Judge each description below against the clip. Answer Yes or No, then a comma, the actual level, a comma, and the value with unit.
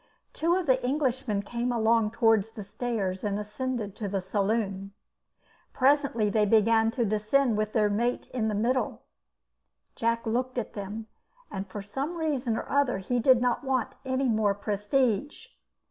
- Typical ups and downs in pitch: Yes, average, 3.7 semitones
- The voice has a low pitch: No, high, 225 Hz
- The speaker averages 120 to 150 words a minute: No, average, 160 wpm